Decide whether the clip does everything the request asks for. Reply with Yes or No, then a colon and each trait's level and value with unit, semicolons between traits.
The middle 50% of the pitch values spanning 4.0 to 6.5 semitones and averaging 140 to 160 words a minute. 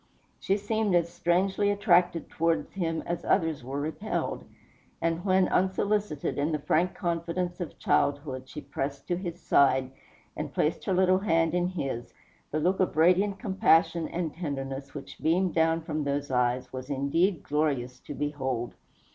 Yes: average, 4.3 semitones; average, 155 wpm